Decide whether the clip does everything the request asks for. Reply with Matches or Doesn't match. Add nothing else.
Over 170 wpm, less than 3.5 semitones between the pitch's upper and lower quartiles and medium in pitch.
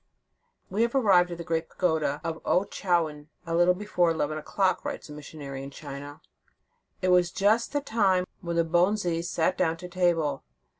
Matches